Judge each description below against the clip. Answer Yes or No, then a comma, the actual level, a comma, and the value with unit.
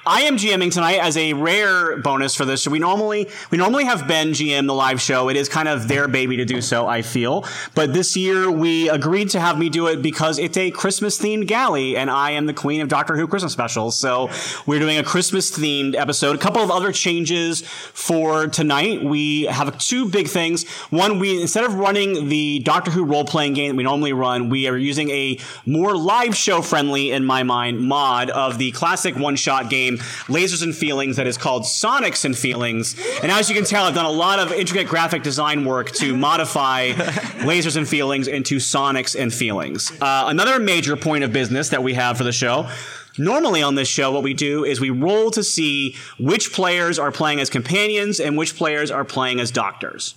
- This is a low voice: No, medium, 150 Hz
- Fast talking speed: Yes, fast, 210 wpm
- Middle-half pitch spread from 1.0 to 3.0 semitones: No, average, 4.3 semitones